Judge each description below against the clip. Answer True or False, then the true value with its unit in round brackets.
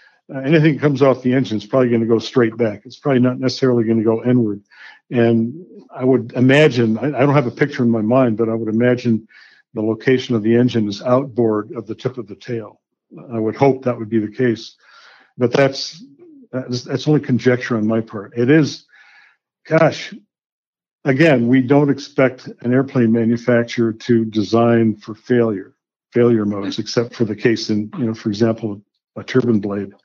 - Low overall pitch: True (120 Hz)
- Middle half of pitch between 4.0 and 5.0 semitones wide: False (2.9 semitones)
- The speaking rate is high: False (185 wpm)